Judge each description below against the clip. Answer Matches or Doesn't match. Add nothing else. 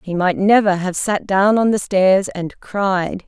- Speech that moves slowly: Doesn't match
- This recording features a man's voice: Doesn't match